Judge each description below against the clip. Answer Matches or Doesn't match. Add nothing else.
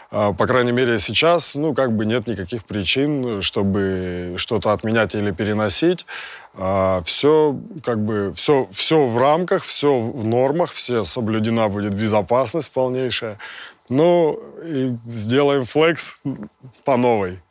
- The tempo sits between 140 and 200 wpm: Doesn't match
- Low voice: Matches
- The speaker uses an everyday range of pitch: Matches